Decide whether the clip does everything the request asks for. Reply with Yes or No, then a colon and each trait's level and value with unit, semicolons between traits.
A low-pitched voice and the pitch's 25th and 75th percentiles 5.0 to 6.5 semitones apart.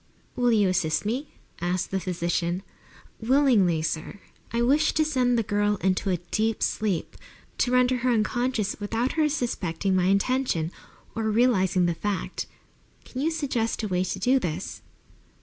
No: high, 215 Hz; average, 5.3 semitones